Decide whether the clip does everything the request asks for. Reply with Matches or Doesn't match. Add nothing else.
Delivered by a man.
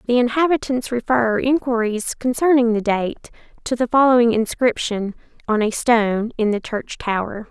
Doesn't match